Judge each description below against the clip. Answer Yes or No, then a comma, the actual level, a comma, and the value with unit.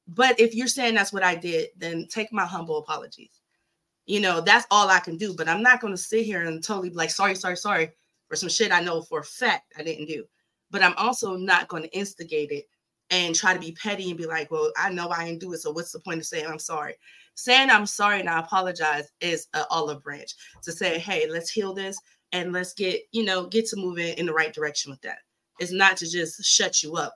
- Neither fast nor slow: No, fast, 255 wpm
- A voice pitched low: No, medium, 180 Hz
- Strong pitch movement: No, average, 3.9 semitones